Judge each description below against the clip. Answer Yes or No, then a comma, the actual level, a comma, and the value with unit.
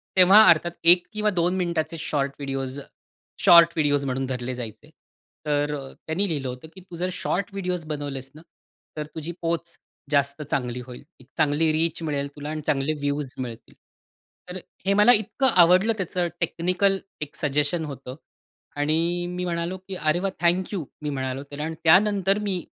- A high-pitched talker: No, medium, 160 Hz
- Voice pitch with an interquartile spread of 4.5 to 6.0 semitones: No, average, 4.1 semitones